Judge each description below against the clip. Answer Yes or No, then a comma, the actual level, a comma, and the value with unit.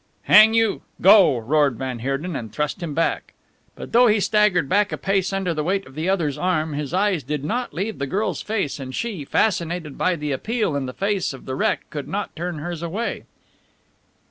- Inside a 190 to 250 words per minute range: Yes, fast, 205 wpm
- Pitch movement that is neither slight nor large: No, wide, 5.7 semitones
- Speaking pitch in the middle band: Yes, medium, 170 Hz